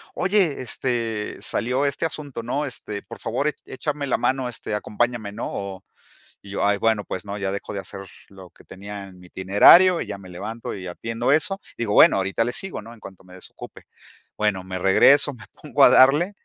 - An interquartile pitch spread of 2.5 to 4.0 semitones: No, wide, 5.5 semitones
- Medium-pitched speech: No, low, 115 Hz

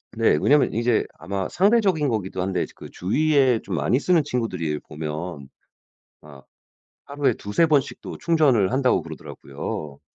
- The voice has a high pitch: No, low, 115 Hz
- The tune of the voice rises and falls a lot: Yes, wide, 8.3 semitones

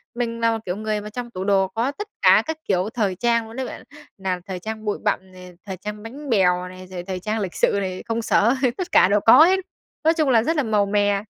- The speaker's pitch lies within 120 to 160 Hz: No, high, 210 Hz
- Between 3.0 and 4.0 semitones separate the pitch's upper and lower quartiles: Yes, average, 3.7 semitones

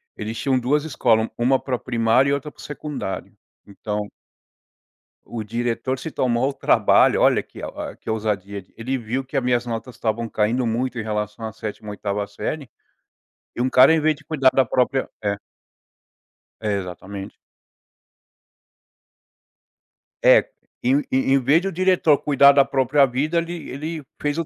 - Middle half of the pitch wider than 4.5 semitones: No, average, 4.1 semitones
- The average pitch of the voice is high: No, low, 125 Hz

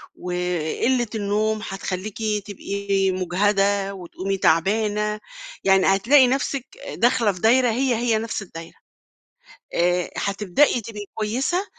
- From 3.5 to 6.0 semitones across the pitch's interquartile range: No, average, 3.1 semitones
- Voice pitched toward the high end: Yes, high, 205 Hz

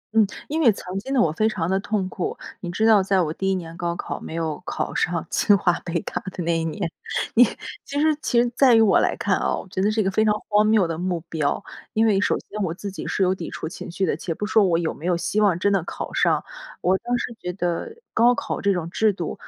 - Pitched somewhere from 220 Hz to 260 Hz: No, high, 190 Hz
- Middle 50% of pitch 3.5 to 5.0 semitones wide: Yes, average, 3.8 semitones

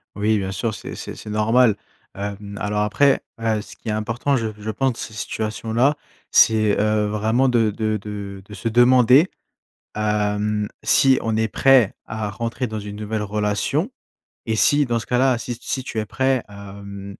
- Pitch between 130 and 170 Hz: No, low, 110 Hz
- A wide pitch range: No, narrow, 2.5 semitones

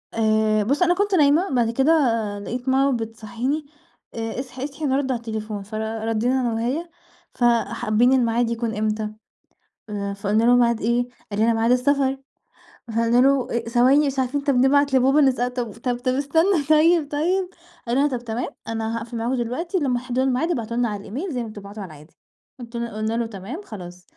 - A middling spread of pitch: Yes, average, 3.4 semitones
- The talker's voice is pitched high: Yes, high, 245 Hz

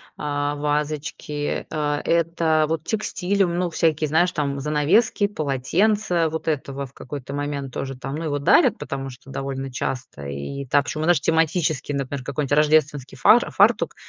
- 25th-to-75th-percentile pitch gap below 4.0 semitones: Yes, average, 2.7 semitones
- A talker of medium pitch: Yes, medium, 150 Hz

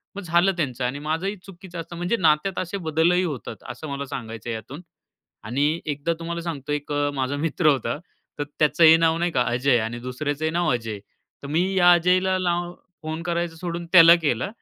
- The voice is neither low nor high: Yes, medium, 160 Hz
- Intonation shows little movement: No, average, 3.8 semitones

